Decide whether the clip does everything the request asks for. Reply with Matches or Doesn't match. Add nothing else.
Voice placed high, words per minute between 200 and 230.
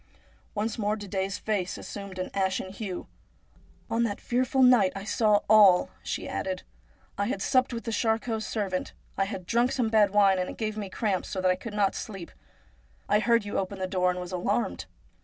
Matches